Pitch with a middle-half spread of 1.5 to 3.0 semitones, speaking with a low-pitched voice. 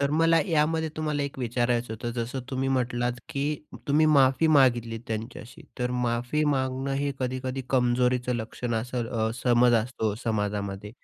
Yes: average, 2.7 semitones; low, 125 Hz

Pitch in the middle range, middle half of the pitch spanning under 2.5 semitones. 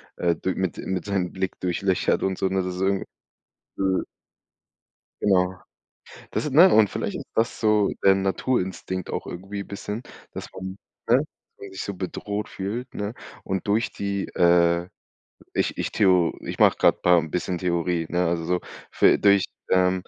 No: very low, 95 Hz; narrow, 1.9 semitones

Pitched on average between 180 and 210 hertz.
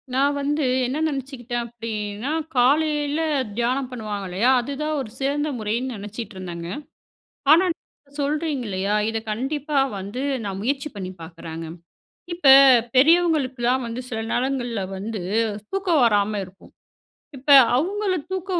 No: very high, 255 Hz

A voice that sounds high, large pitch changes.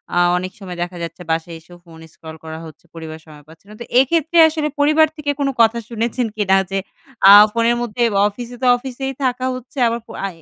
Yes: high, 230 Hz; wide, 7.1 semitones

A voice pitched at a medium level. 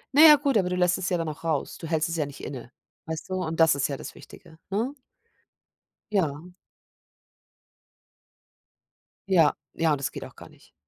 Yes: medium, 165 Hz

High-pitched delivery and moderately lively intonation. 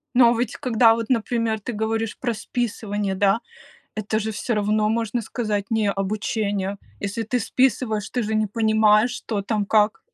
No: high, 220 Hz; narrow, 1.8 semitones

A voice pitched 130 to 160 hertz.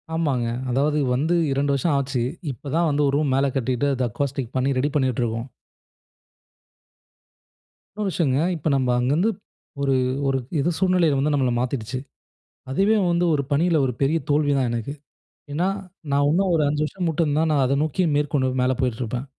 Yes: medium, 140 Hz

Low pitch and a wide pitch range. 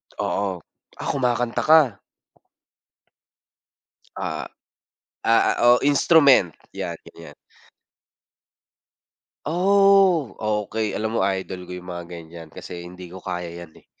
Yes: low, 100 Hz; wide, 8.1 semitones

